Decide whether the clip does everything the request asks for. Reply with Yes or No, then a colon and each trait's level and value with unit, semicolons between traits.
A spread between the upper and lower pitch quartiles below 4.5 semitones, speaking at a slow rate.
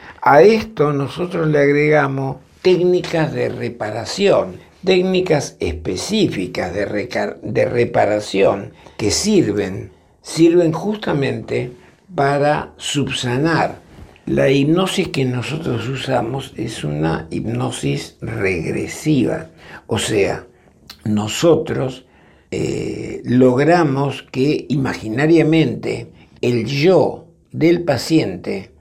No: wide, 5.4 semitones; slow, 85 wpm